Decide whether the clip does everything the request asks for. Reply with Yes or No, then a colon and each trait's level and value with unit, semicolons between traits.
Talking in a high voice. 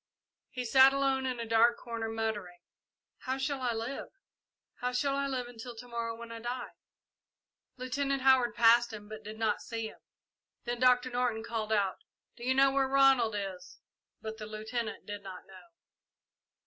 Yes: high, 235 Hz